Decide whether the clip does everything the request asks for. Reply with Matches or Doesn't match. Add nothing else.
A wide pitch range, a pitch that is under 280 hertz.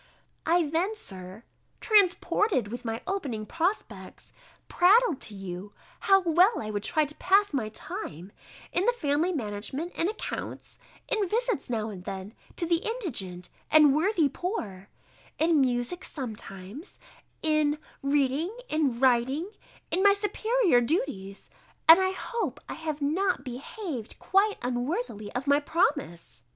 Doesn't match